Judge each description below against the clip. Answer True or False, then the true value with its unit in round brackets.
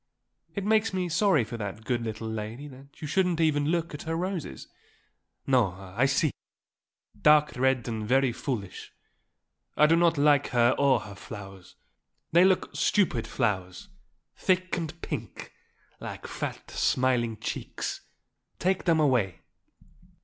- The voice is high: False (135 Hz)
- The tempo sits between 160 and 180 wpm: False (140 wpm)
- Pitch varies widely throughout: True (6.4 semitones)